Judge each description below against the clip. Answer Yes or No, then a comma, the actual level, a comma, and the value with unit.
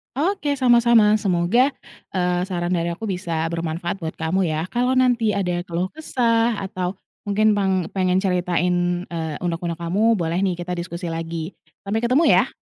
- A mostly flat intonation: No, average, 4.1 semitones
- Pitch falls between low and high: Yes, medium, 180 Hz